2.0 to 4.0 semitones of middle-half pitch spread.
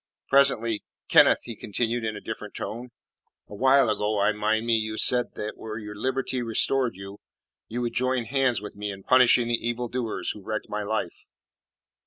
Yes: average, 2.7 semitones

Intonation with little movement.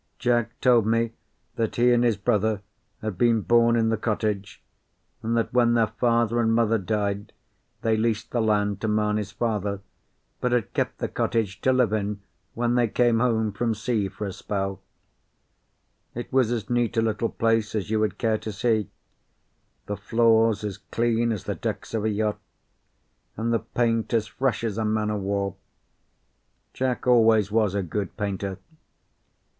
Yes: narrow, 2.0 semitones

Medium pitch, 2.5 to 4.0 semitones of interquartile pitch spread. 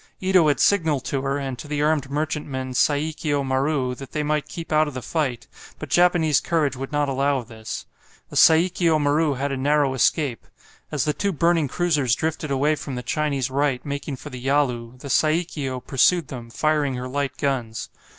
Yes: medium, 145 Hz; average, 2.8 semitones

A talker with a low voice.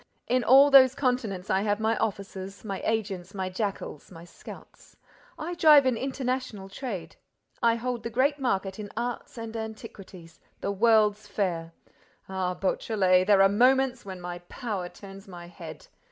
No: high, 210 Hz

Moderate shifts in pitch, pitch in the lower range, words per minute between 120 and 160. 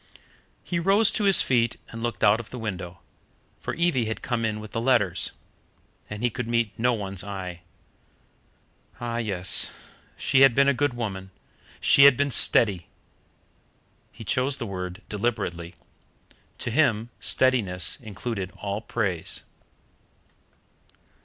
Yes: average, 4.1 semitones; low, 115 Hz; average, 140 wpm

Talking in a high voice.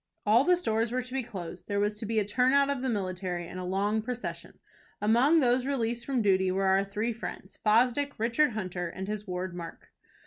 Yes: high, 215 Hz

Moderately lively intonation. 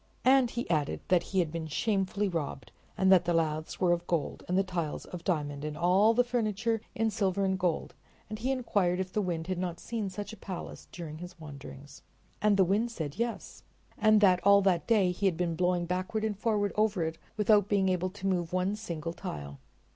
Yes: average, 3.6 semitones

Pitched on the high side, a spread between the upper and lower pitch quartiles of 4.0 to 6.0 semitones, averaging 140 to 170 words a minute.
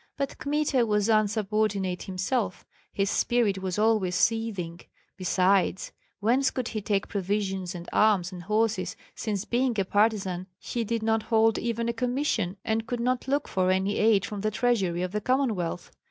No: high, 215 Hz; average, 3.3 semitones; average, 165 wpm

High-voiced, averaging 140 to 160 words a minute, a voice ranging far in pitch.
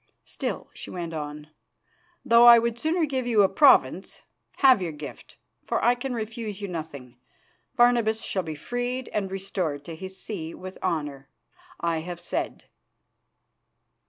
Yes: high, 195 Hz; average, 150 wpm; wide, 6.7 semitones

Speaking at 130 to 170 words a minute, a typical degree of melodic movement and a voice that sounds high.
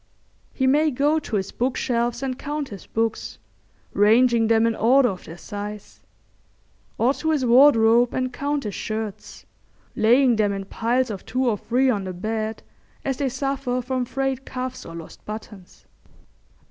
Yes: average, 160 wpm; average, 3.5 semitones; high, 240 Hz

